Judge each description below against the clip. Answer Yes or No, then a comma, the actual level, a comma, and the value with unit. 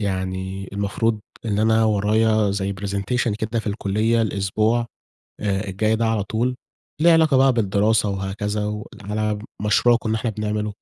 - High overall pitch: No, low, 105 Hz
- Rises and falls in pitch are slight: Yes, narrow, 1.9 semitones